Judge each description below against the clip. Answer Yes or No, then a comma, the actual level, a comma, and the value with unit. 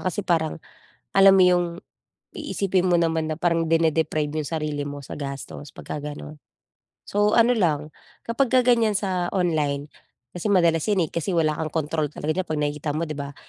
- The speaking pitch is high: No, medium, 165 Hz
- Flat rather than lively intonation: No, average, 3.7 semitones